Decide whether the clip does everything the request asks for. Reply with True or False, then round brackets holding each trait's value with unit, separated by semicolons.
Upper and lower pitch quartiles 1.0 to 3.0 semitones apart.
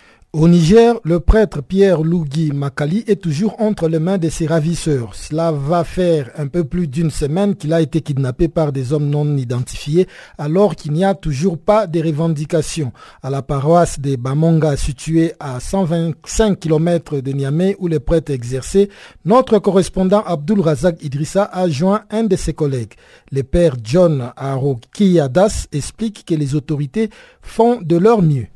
False (4.2 semitones)